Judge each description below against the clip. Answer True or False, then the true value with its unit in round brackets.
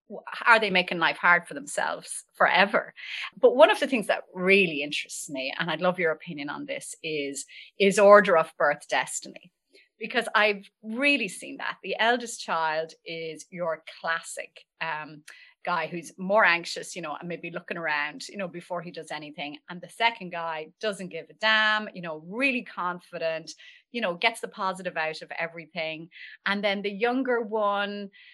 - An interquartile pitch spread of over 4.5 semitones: True (4.9 semitones)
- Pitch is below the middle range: False (180 Hz)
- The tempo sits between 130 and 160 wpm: False (175 wpm)